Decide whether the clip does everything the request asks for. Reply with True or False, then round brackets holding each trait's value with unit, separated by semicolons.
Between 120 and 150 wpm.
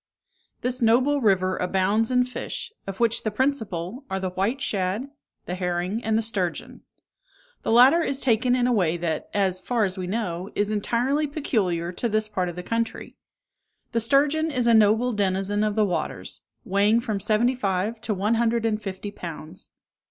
False (180 wpm)